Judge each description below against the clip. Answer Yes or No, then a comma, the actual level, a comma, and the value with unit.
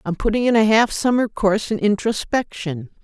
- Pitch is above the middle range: Yes, high, 210 Hz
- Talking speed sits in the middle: Yes, average, 180 wpm